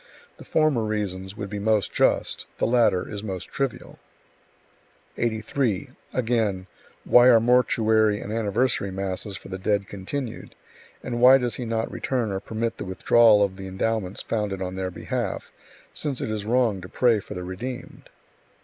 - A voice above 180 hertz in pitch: No, low, 110 Hz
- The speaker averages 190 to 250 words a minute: No, average, 160 wpm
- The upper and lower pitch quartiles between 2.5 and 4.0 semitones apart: Yes, average, 3.6 semitones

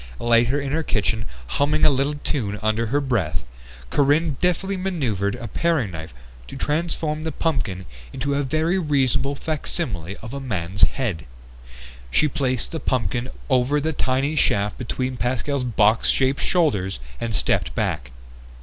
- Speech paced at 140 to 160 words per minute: Yes, average, 150 wpm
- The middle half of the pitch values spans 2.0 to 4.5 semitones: No, average, 5.3 semitones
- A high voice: No, low, 130 Hz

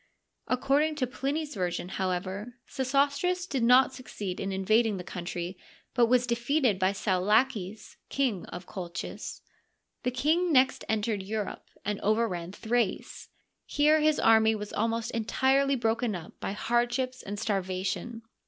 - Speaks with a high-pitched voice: Yes, high, 225 Hz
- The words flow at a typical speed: No, slow, 130 wpm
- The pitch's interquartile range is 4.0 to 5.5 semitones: Yes, average, 5.2 semitones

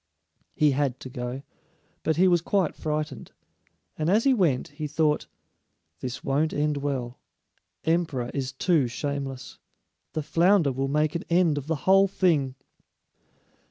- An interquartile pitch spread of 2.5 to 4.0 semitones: Yes, average, 3.7 semitones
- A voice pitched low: No, medium, 150 Hz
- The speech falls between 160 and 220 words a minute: No, average, 145 wpm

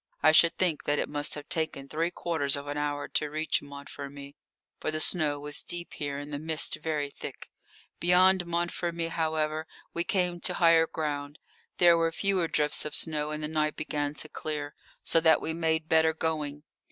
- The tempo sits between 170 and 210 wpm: Yes, average, 190 wpm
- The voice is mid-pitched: Yes, medium, 155 Hz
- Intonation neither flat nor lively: No, narrow, 2.2 semitones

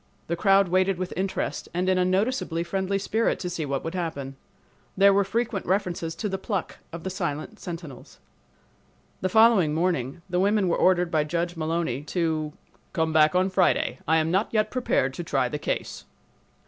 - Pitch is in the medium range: Yes, medium, 180 Hz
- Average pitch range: Yes, average, 3.1 semitones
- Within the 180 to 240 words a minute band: Yes, average, 185 wpm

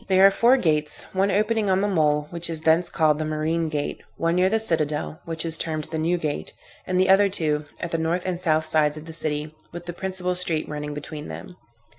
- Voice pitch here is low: No, medium, 165 Hz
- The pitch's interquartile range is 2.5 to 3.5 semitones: Yes, average, 3.1 semitones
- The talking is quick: Yes, fast, 230 wpm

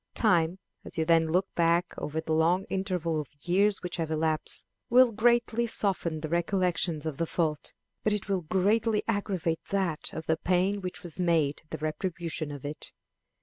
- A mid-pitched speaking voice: Yes, medium, 175 Hz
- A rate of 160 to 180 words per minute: Yes, average, 175 wpm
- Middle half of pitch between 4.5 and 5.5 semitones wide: No, average, 3.4 semitones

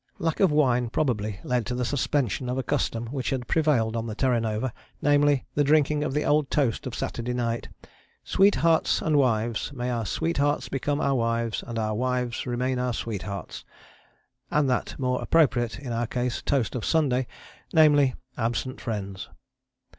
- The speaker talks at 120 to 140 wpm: No, average, 170 wpm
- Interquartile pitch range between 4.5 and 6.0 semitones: No, average, 3.7 semitones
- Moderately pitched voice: No, low, 125 Hz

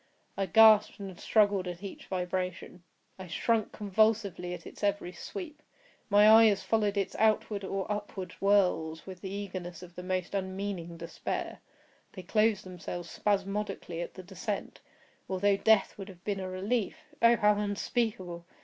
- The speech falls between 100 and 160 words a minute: Yes, average, 150 wpm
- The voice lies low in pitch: No, high, 195 Hz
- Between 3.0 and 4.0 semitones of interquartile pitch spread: No, narrow, 2.4 semitones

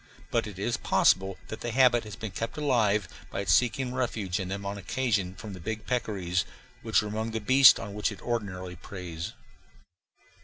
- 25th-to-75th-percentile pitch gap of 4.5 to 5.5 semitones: No, average, 3.7 semitones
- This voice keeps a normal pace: Yes, average, 190 wpm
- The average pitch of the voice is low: Yes, low, 105 Hz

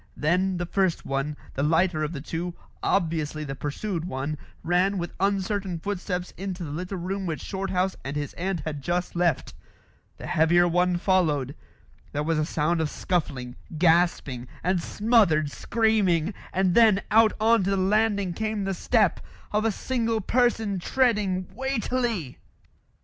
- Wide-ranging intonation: No, average, 4.0 semitones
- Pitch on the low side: No, medium, 180 Hz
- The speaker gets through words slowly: No, average, 155 wpm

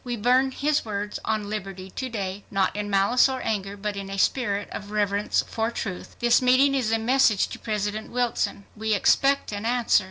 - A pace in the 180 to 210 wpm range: Yes, average, 195 wpm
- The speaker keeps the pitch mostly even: No, average, 3.4 semitones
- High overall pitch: Yes, high, 215 Hz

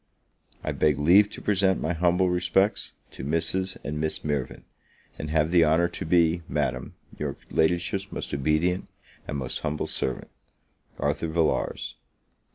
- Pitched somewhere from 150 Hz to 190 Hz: No, very low, 80 Hz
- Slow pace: No, average, 145 wpm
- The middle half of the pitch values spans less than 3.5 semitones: Yes, average, 2.9 semitones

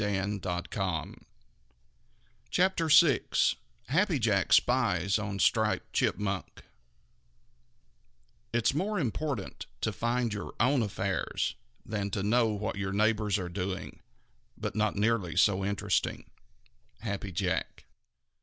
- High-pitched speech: No, low, 105 Hz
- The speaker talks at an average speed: No, slow, 100 wpm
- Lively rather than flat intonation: No, average, 3.9 semitones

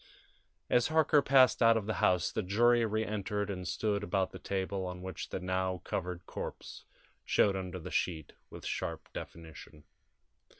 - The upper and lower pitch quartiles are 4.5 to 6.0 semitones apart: No, average, 3.2 semitones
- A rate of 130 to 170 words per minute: Yes, average, 160 wpm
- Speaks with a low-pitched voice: Yes, very low, 95 Hz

